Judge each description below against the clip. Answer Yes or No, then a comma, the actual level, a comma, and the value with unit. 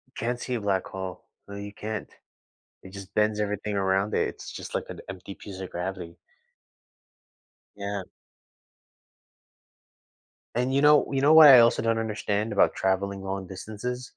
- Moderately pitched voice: No, low, 100 Hz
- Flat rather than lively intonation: No, average, 3.1 semitones